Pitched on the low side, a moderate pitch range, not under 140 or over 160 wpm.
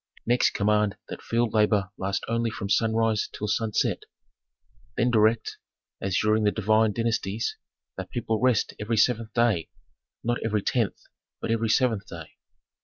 No: low, 110 Hz; narrow, 1.7 semitones; average, 145 wpm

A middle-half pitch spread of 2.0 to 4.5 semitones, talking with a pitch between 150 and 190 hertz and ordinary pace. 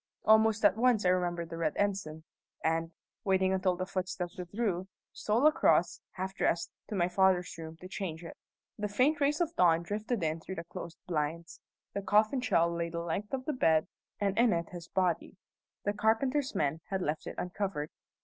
Yes: average, 3.8 semitones; medium, 185 Hz; average, 190 wpm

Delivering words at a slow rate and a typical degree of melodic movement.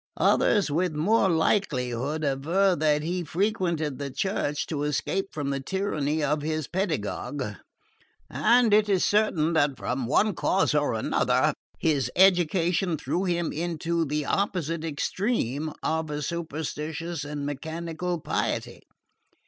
Yes: slow, 130 wpm; average, 3.7 semitones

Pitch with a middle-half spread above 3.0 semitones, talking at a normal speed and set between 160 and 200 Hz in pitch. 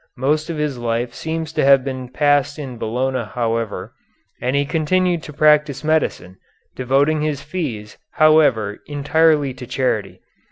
No: average, 3.7 semitones; average, 145 wpm; medium, 140 Hz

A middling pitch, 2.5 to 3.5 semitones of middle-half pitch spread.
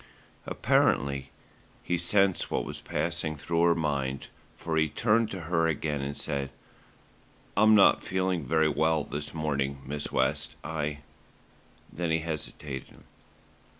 No: very low, 80 Hz; average, 3.0 semitones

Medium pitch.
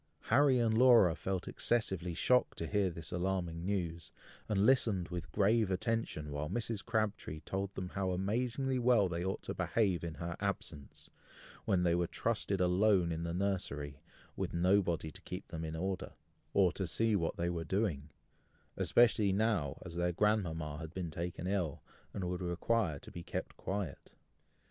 No: very low, 95 Hz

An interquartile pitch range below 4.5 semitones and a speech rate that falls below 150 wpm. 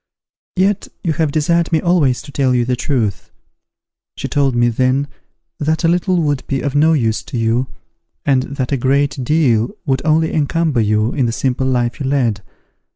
No: average, 4.0 semitones; average, 185 wpm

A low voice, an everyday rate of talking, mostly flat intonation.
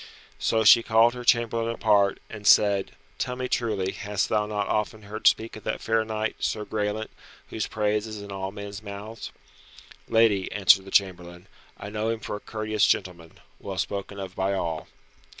Yes: low, 105 Hz; average, 180 wpm; narrow, 1.9 semitones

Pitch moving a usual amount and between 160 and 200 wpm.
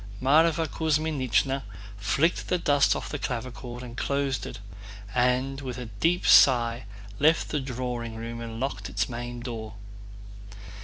No: average, 3.3 semitones; average, 140 wpm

